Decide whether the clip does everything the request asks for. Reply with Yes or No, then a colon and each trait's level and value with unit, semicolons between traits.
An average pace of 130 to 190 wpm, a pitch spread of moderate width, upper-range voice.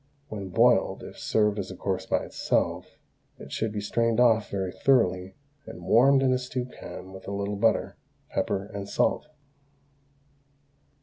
No: average, 160 wpm; average, 3.3 semitones; low, 105 Hz